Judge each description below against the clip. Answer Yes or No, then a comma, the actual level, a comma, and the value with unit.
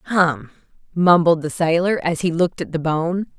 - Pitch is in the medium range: Yes, medium, 170 Hz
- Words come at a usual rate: Yes, average, 175 wpm